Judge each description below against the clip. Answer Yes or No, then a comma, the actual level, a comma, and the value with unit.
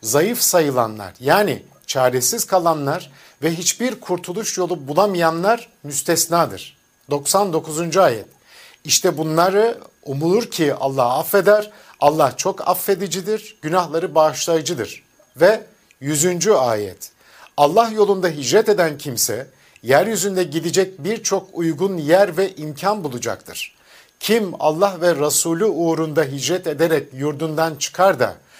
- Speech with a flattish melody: No, average, 4.6 semitones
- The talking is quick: No, average, 105 wpm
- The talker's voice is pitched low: No, medium, 170 Hz